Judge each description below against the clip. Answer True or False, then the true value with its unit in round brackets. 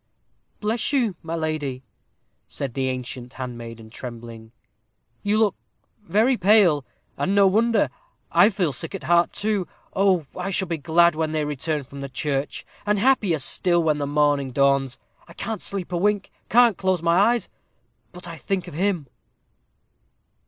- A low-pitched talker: False (170 Hz)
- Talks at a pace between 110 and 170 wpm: True (160 wpm)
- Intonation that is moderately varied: False (6.2 semitones)